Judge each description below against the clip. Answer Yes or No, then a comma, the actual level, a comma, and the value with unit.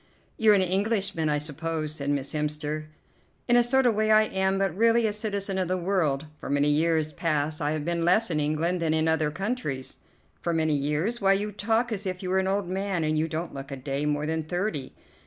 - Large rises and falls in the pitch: No, average, 4.8 semitones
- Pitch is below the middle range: No, medium, 170 Hz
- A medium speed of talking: No, fast, 230 wpm